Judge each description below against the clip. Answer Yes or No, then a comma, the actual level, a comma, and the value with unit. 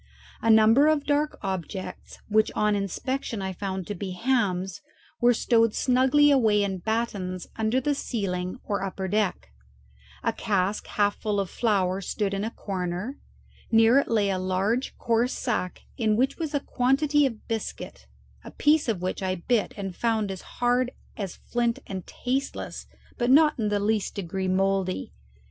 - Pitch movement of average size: Yes, average, 4.3 semitones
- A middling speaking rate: Yes, average, 165 wpm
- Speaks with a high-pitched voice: Yes, high, 215 Hz